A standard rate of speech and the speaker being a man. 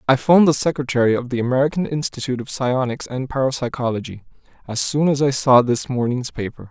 Yes: average, 180 wpm; male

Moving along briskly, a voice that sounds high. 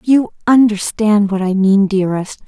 No: average, 145 wpm; high, 205 Hz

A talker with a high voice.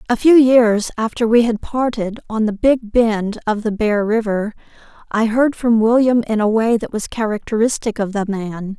Yes: high, 225 Hz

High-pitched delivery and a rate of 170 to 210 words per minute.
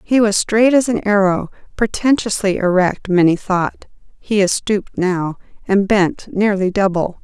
No: high, 200 Hz; average, 140 wpm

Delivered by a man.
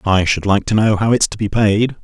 Yes: male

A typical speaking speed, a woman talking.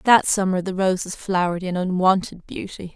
Yes: average, 160 wpm; female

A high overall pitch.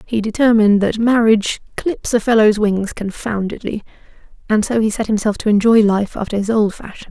Yes: high, 215 Hz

